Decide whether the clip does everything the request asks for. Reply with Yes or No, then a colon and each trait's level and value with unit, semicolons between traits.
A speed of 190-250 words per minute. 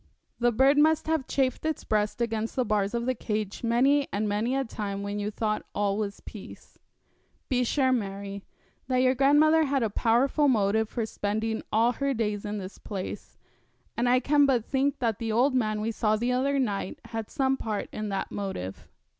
Yes: average, 195 wpm